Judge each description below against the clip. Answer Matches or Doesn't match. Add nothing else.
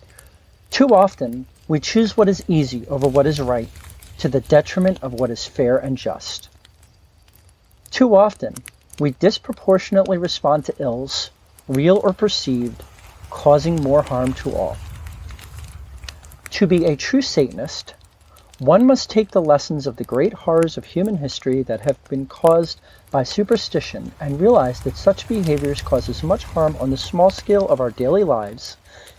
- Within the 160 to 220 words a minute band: Doesn't match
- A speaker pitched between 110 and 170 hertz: Matches